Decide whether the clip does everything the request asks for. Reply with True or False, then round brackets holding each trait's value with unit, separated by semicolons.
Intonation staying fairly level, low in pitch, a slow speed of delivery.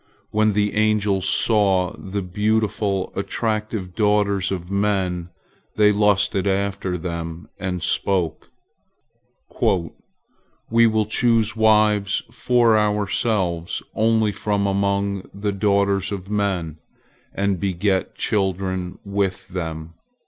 True (2.1 semitones; 100 Hz; 100 wpm)